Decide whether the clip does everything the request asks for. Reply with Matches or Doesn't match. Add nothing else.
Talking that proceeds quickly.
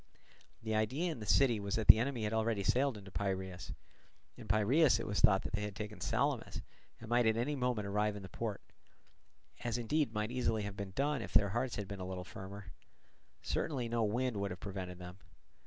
Matches